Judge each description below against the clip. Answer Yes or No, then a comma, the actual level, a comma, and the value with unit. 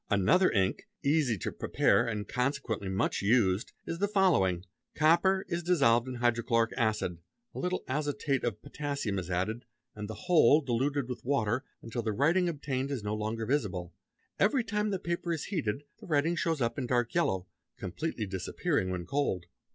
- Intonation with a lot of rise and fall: Yes, wide, 6.7 semitones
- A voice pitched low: Yes, low, 125 Hz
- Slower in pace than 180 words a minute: Yes, average, 170 wpm